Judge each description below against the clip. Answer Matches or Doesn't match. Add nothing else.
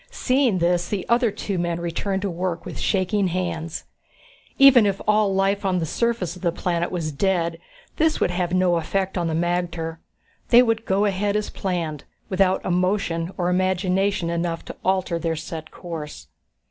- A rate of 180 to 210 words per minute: Doesn't match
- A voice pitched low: Doesn't match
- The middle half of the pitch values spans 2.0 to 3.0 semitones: Matches